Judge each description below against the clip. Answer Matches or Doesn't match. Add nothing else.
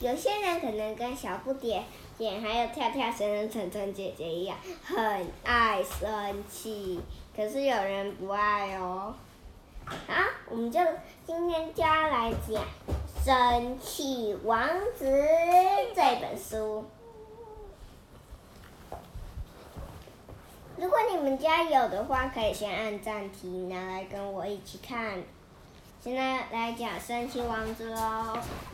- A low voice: Doesn't match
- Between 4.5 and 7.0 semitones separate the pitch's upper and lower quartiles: Matches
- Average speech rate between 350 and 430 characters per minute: Doesn't match